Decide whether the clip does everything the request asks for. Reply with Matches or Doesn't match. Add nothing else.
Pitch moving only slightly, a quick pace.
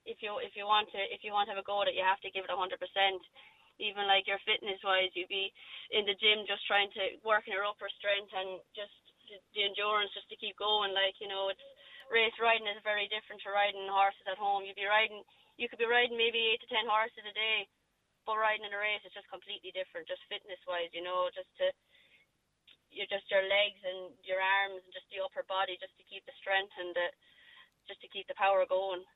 Matches